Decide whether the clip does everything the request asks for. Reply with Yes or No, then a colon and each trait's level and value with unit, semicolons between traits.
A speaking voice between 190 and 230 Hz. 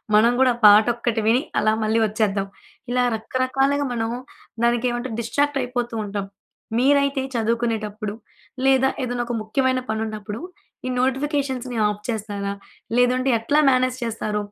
No: high, 240 Hz